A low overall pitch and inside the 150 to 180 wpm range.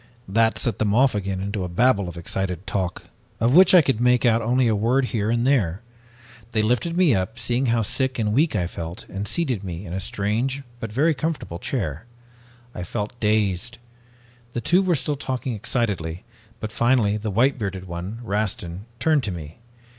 No: low, 110 Hz; average, 190 wpm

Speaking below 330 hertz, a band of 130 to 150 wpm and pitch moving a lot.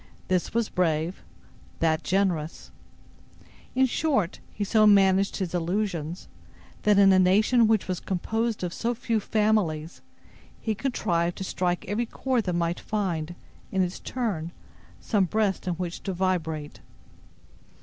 No: high, 190 Hz; average, 140 wpm; average, 3.8 semitones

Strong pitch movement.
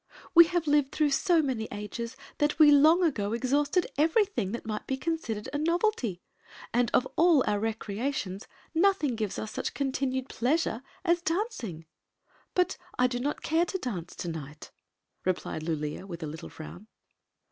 Yes: wide, 7.6 semitones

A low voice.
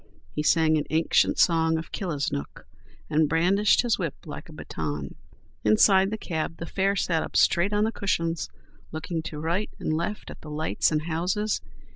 No: medium, 165 Hz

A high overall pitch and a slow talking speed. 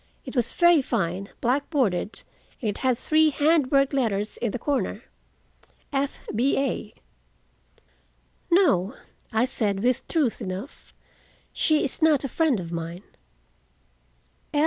Yes: very high, 255 Hz; slow, 125 wpm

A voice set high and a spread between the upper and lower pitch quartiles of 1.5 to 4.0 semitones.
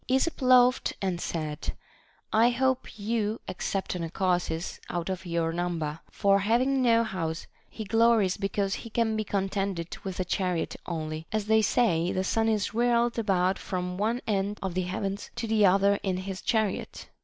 Yes: high, 195 Hz; average, 3.7 semitones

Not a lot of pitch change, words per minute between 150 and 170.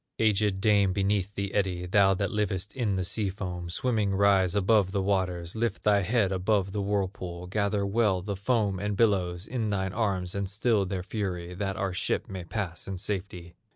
No: narrow, 2.0 semitones; average, 190 wpm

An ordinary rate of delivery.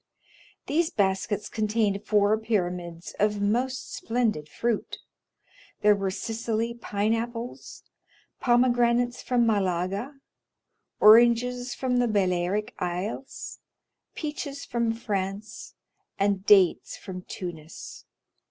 No: slow, 95 wpm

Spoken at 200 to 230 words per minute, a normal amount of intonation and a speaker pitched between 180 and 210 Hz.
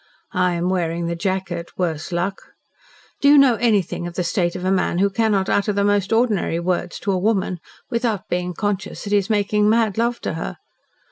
Yes: fast, 205 wpm; average, 3.1 semitones; high, 190 Hz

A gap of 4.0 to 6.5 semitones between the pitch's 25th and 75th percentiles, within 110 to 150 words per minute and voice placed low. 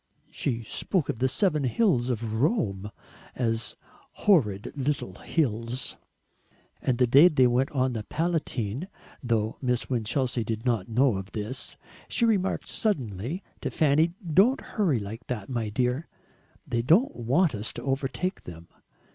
Yes: wide, 5.4 semitones; average, 145 wpm; low, 125 Hz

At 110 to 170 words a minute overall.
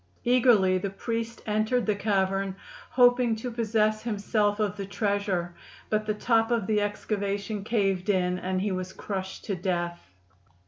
Yes: average, 150 wpm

